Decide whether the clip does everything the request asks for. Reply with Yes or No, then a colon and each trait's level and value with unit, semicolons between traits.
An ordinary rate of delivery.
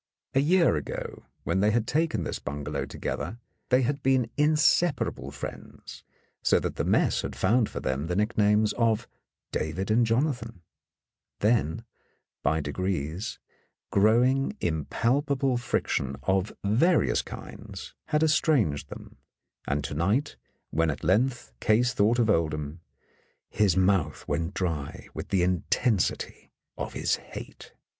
No: slow, 130 wpm